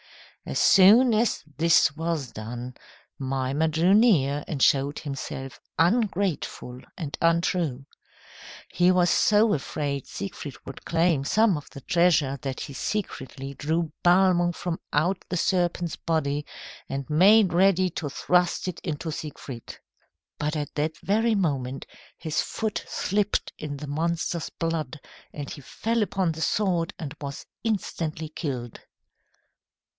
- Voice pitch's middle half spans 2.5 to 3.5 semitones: No, average, 4.4 semitones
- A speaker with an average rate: No, slow, 130 wpm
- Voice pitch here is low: No, medium, 160 Hz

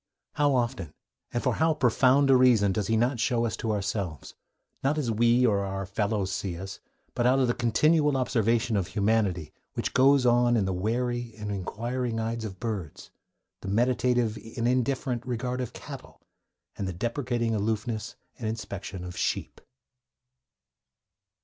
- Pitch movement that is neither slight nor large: Yes, average, 3.5 semitones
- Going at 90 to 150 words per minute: No, average, 160 wpm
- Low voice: Yes, low, 115 Hz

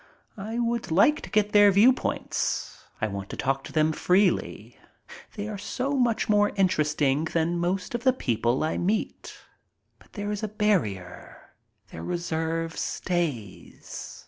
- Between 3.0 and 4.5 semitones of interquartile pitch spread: No, wide, 5.5 semitones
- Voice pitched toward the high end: No, medium, 180 Hz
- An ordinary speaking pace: Yes, average, 145 wpm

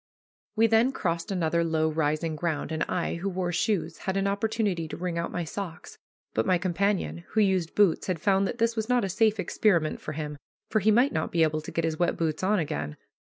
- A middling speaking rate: No, fast, 225 wpm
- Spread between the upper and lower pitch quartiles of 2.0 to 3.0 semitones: No, average, 4.1 semitones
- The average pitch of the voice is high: No, medium, 175 Hz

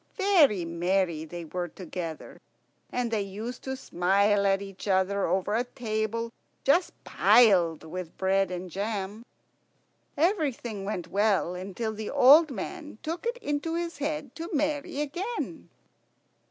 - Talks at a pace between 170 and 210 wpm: No, slow, 135 wpm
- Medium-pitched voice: No, high, 215 Hz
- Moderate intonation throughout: No, wide, 7.2 semitones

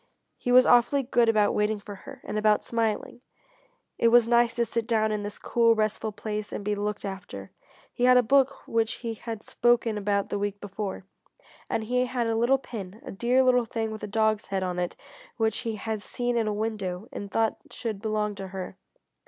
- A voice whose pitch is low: No, high, 220 Hz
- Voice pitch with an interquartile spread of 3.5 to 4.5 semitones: No, narrow, 2.5 semitones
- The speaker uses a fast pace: Yes, fast, 210 wpm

